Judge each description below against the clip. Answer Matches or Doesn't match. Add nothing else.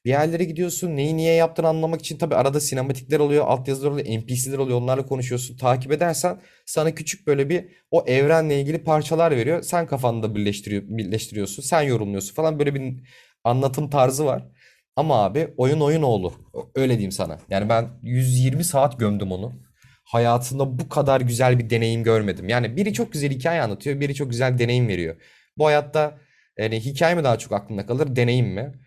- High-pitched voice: Doesn't match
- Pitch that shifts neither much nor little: Matches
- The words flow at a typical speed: Doesn't match